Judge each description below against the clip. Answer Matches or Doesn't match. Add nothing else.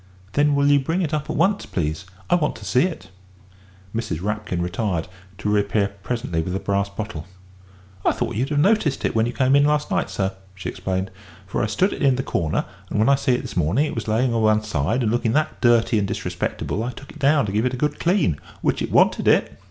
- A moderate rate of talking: Doesn't match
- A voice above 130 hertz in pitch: Doesn't match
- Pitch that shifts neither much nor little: Doesn't match